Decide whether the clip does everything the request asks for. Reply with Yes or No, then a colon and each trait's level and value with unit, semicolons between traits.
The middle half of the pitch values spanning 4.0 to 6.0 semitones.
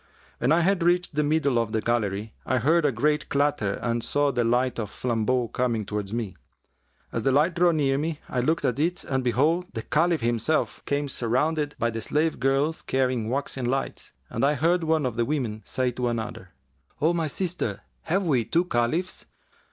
Yes: average, 5.0 semitones